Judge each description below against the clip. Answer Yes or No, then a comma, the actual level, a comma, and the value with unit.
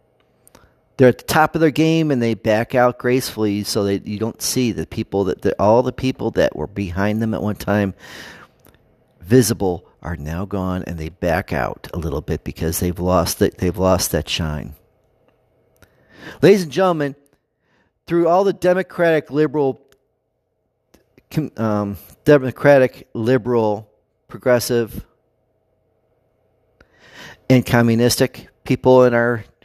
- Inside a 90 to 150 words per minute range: Yes, slow, 135 wpm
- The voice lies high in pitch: No, low, 115 Hz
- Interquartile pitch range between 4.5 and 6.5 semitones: Yes, average, 4.9 semitones